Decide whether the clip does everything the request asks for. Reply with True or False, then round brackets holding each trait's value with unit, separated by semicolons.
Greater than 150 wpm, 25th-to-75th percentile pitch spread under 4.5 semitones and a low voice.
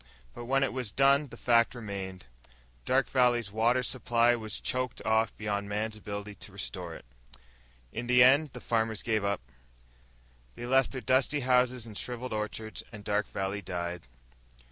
True (160 wpm; 3.6 semitones; 115 Hz)